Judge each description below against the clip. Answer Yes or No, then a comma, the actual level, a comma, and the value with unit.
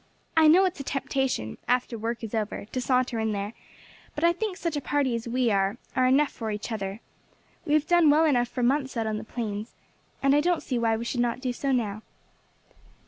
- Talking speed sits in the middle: No, fast, 225 wpm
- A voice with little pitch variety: No, average, 4.6 semitones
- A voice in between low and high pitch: No, very high, 250 Hz